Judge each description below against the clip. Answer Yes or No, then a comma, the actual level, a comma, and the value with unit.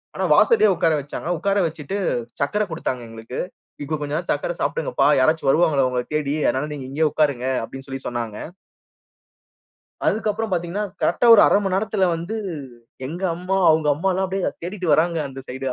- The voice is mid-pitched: Yes, medium, 160 Hz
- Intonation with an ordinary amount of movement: No, wide, 6.0 semitones